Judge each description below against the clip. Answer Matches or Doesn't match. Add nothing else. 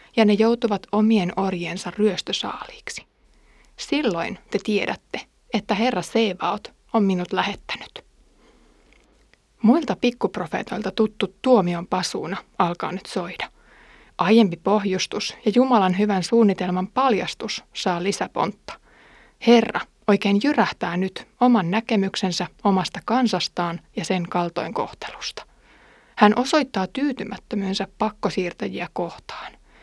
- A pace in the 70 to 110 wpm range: Matches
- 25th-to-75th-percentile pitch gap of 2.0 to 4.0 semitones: Matches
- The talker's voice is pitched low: Doesn't match